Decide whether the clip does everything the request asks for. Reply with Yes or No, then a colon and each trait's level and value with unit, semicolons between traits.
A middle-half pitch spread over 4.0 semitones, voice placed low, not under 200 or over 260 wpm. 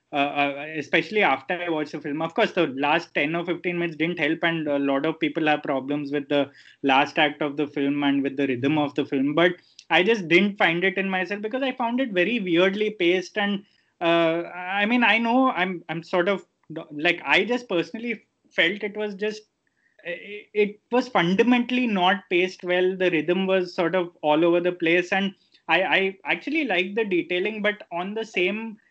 No: average, 4.4 semitones; medium, 180 Hz; fast, 205 wpm